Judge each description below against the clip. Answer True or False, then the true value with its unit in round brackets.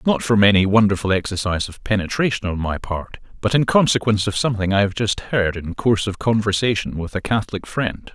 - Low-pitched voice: True (105 Hz)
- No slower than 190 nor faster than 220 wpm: True (200 wpm)